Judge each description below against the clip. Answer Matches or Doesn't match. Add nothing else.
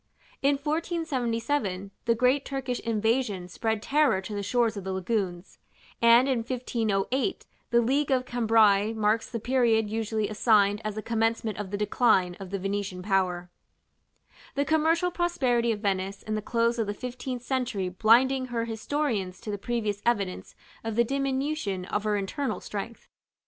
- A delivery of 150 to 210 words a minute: Matches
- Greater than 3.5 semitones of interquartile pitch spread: Matches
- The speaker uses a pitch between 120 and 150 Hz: Doesn't match